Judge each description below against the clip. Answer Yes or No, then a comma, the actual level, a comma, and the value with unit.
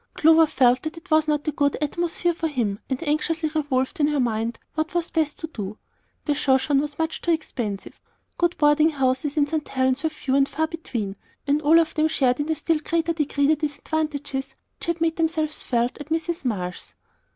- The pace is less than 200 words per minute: No, fast, 205 wpm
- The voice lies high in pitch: Yes, very high, 300 Hz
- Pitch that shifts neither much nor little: Yes, average, 3.2 semitones